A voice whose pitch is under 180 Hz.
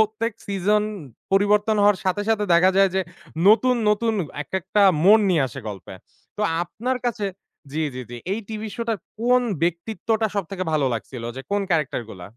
No: high, 205 Hz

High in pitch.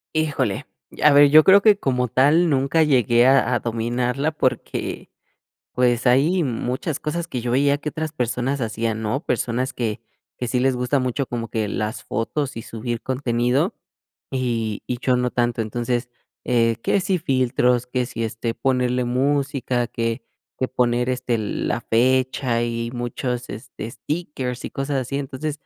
No: low, 125 Hz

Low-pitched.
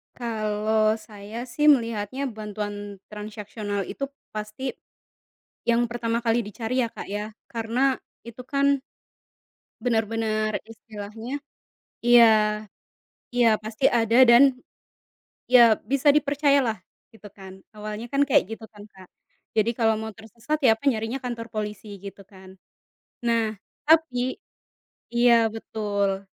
No: high, 225 Hz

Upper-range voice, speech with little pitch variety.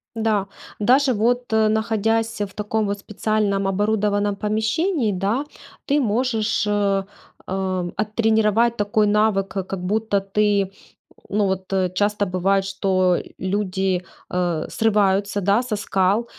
Yes: high, 205 Hz; narrow, 2.2 semitones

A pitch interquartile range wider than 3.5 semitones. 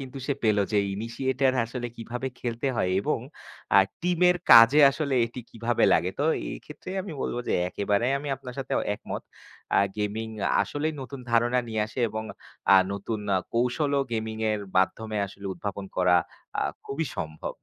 Yes: average, 4.1 semitones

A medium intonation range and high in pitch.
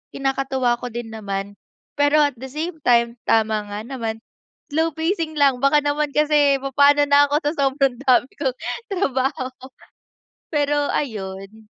Yes: average, 3.5 semitones; very high, 275 Hz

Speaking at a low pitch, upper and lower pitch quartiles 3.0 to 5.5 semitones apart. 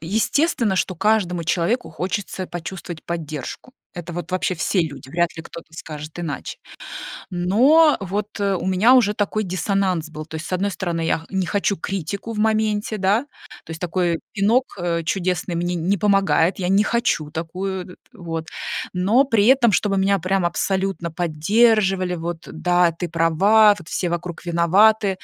No: medium, 185 Hz; average, 3.4 semitones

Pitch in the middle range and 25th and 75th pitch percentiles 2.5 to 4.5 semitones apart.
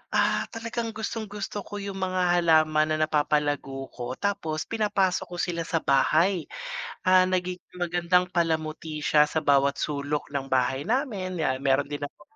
Yes: medium, 165 Hz; average, 3.9 semitones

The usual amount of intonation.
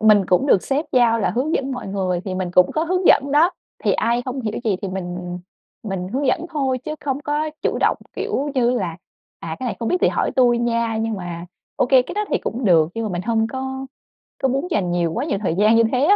No: wide, 5.9 semitones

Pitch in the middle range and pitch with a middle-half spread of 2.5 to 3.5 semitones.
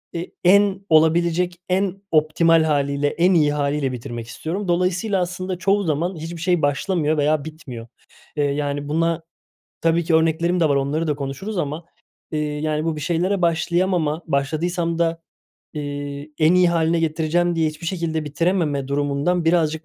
Yes: medium, 160 Hz; average, 2.9 semitones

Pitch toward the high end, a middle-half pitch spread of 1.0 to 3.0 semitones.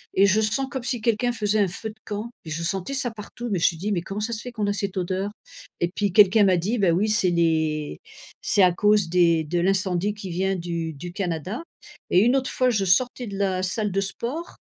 No: high, 195 Hz; average, 3.6 semitones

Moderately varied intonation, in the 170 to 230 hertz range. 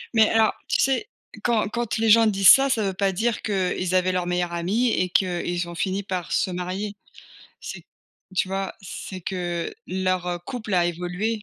Yes: average, 3.4 semitones; high, 190 Hz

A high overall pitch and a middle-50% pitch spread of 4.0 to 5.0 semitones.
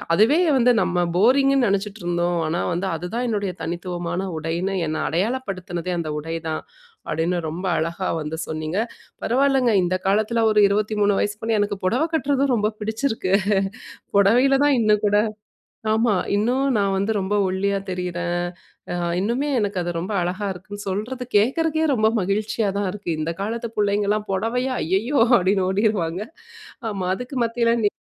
Yes: high, 205 Hz; average, 4.3 semitones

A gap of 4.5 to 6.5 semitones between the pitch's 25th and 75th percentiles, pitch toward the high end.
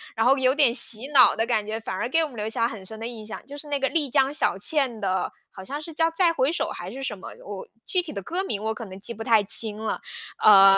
Yes: average, 5.0 semitones; high, 235 Hz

